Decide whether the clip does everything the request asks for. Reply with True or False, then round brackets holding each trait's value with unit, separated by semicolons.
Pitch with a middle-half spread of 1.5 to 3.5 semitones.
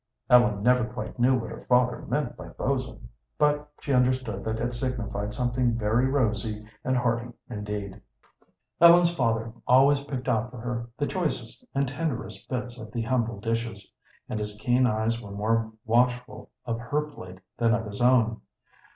True (2.5 semitones)